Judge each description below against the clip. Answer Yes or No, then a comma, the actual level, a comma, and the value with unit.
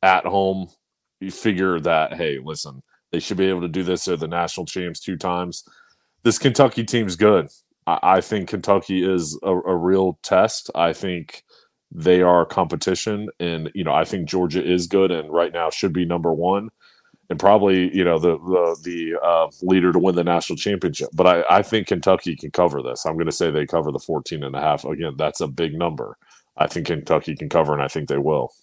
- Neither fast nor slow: No, fast, 210 wpm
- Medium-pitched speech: No, very low, 90 Hz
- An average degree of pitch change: No, narrow, 1.6 semitones